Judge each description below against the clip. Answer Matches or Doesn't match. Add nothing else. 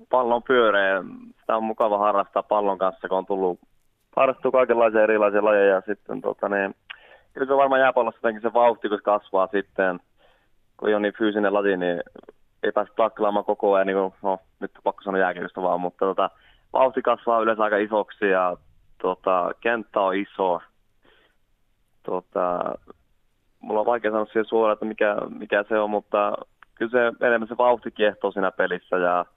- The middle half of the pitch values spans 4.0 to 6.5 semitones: Doesn't match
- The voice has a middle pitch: Doesn't match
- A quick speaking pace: Matches